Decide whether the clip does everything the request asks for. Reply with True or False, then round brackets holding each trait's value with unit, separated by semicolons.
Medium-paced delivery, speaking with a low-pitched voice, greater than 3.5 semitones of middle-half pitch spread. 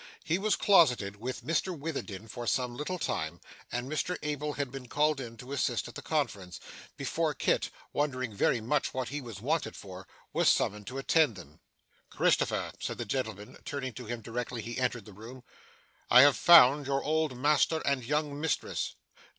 True (180 wpm; 130 Hz; 4.3 semitones)